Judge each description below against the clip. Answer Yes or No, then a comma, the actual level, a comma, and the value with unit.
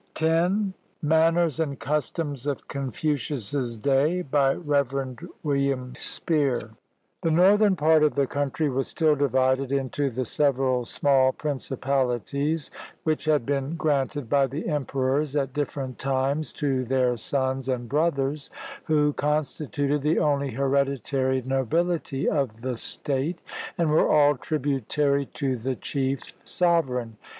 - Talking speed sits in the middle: No, slow, 125 wpm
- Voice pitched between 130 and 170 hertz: Yes, medium, 140 Hz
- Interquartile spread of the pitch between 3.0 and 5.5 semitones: No, narrow, 2.4 semitones